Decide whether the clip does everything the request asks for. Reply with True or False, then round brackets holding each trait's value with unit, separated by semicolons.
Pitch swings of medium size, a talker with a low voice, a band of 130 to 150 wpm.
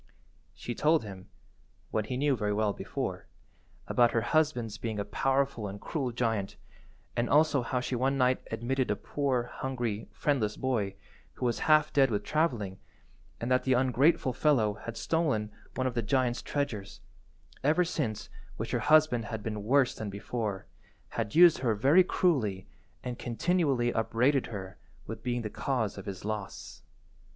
False (4.3 semitones; 120 Hz; 160 wpm)